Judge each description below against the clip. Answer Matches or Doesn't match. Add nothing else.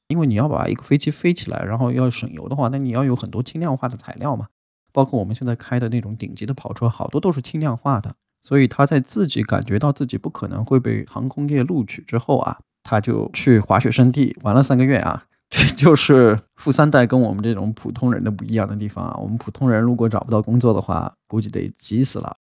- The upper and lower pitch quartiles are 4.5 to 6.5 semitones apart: Doesn't match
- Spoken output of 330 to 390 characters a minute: Matches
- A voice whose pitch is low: Matches